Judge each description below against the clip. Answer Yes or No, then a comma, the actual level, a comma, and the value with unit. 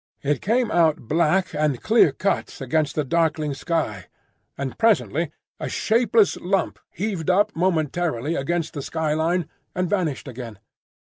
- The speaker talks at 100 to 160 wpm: Yes, average, 140 wpm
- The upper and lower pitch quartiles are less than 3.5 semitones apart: No, average, 4.1 semitones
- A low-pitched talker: No, medium, 160 Hz